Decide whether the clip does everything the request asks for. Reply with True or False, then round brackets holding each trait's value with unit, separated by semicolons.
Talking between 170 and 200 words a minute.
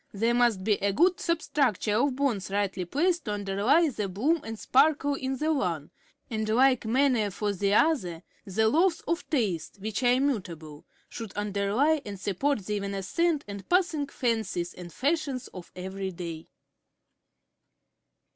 False (155 wpm)